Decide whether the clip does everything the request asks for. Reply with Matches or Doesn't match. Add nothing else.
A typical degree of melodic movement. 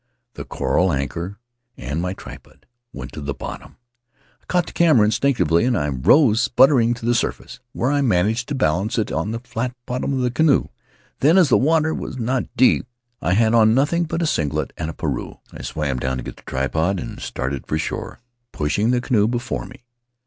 Doesn't match